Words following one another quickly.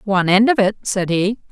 Yes: fast, 235 wpm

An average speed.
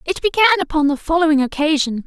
Yes: average, 175 wpm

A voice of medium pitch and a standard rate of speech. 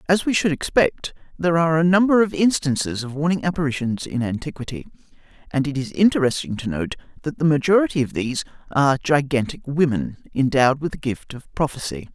Yes: medium, 150 Hz; average, 175 wpm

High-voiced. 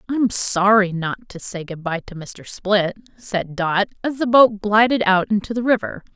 Yes: high, 200 Hz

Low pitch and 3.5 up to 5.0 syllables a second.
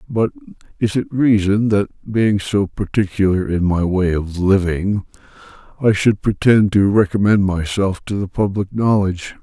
Yes: low, 100 Hz; 4.5 syllables/s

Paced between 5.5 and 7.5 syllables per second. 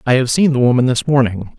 Yes: 6.3 syllables/s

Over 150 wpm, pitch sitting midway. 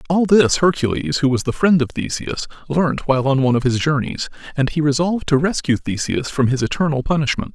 Yes: fast, 205 wpm; medium, 145 Hz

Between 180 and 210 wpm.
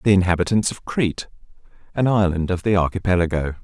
No: average, 150 wpm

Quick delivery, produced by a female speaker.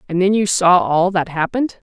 Yes: fast, 220 wpm; female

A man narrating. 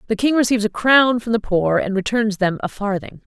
No: female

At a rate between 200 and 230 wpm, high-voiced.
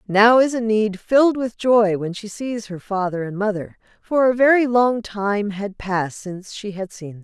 Yes: fast, 205 wpm; high, 210 Hz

